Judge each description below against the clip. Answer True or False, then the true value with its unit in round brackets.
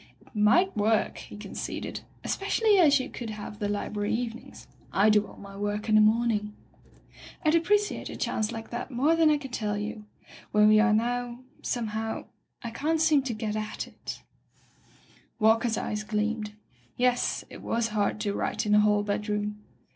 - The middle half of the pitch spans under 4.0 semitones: True (2.7 semitones)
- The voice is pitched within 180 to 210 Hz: False (220 Hz)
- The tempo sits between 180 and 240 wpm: True (185 wpm)